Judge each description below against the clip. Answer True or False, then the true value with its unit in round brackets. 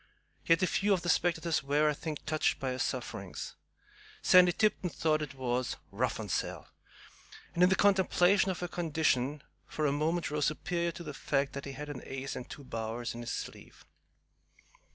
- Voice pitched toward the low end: False (155 Hz)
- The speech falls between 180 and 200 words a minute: True (190 wpm)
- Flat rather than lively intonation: False (4.2 semitones)